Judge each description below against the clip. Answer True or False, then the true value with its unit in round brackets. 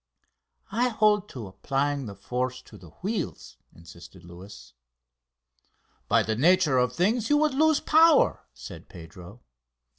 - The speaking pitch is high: False (135 Hz)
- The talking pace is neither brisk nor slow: False (130 wpm)